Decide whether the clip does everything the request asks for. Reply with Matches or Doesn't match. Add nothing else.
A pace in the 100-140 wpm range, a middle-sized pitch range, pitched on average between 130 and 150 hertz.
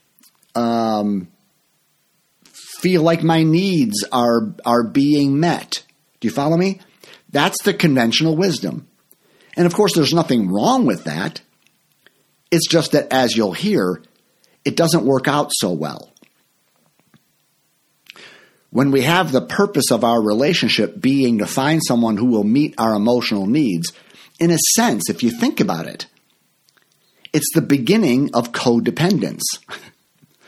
Doesn't match